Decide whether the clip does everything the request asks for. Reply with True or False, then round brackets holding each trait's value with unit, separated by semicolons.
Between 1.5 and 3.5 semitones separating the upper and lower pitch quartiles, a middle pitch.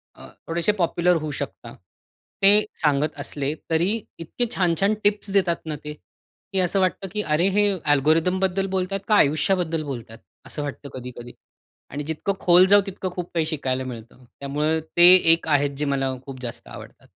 False (4.6 semitones; 165 Hz)